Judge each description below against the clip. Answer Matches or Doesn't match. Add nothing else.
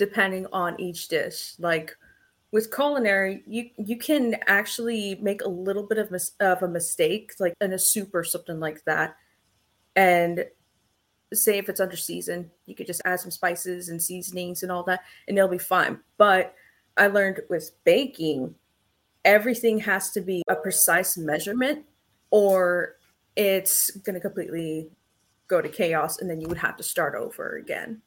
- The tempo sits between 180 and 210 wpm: Doesn't match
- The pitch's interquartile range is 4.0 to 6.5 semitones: Doesn't match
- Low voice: Doesn't match